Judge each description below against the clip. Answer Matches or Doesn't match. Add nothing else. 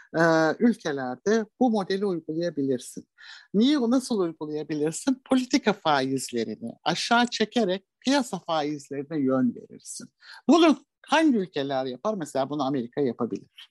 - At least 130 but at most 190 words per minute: Doesn't match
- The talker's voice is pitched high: Doesn't match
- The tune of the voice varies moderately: Doesn't match